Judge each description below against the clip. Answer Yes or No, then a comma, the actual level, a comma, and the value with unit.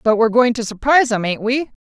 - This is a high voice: Yes, high, 235 Hz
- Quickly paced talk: Yes, fast, 255 wpm